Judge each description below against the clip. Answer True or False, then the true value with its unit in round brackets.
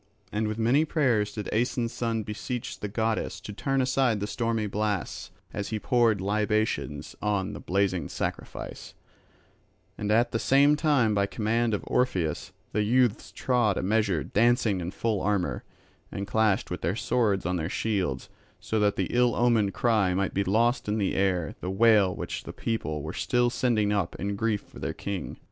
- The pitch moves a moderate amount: True (3.0 semitones)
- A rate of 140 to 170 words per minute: False (180 wpm)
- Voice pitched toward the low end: True (105 Hz)